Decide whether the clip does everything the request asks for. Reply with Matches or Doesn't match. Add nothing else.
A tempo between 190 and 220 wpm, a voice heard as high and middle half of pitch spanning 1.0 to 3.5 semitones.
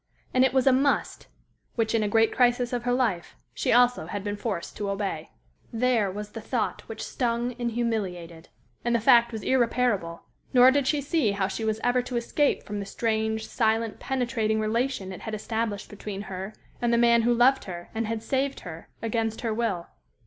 Matches